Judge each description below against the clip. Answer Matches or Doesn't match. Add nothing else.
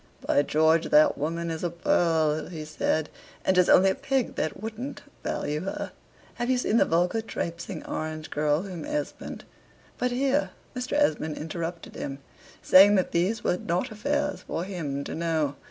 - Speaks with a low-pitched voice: Doesn't match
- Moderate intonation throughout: Doesn't match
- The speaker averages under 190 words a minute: Matches